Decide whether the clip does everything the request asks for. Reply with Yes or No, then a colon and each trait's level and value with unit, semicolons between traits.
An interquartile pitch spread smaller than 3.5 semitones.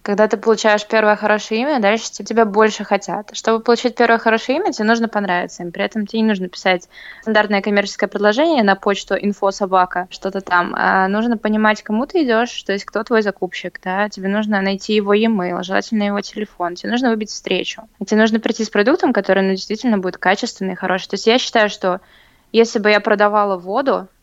Yes: narrow, 2.4 semitones